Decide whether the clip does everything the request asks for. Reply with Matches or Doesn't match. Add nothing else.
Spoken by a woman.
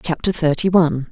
Matches